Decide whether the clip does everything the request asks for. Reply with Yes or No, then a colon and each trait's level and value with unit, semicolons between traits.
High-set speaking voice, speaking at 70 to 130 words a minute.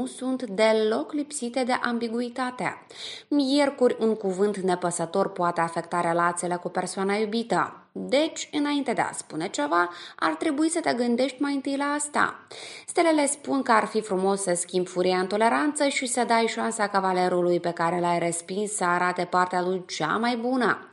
No: high, 220 Hz; average, 165 wpm